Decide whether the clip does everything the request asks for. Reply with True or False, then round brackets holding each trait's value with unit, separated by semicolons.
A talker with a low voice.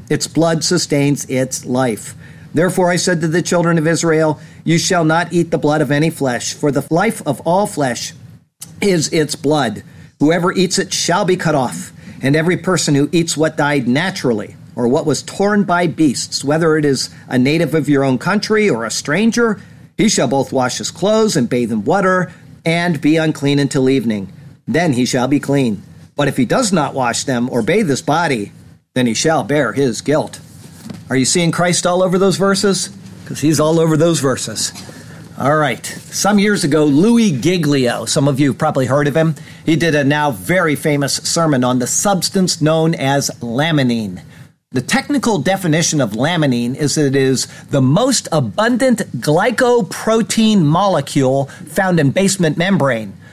False (155 Hz)